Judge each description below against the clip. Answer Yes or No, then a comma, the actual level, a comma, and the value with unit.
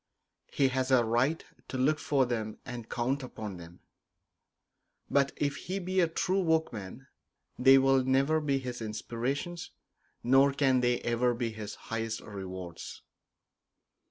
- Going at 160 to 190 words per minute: No, average, 140 wpm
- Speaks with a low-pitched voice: Yes, low, 130 Hz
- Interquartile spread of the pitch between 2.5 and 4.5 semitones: Yes, average, 3.6 semitones